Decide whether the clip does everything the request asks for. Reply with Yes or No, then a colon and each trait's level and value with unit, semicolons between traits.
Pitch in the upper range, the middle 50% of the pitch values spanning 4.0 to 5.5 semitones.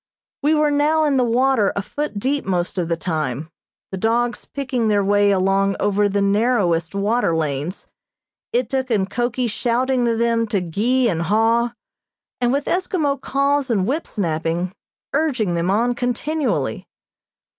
Yes: high, 230 Hz; average, 5.2 semitones